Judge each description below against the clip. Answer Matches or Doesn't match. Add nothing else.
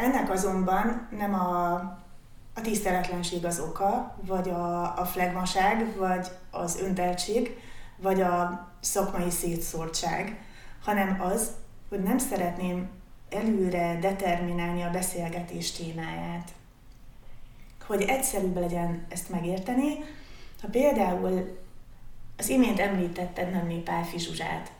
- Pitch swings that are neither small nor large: Doesn't match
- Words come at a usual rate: Doesn't match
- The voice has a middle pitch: Matches